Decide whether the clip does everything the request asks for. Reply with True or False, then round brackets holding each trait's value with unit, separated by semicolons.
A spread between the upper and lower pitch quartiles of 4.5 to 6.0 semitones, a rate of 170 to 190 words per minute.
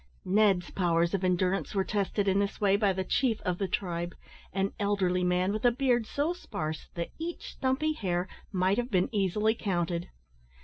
False (3.2 semitones; 180 wpm)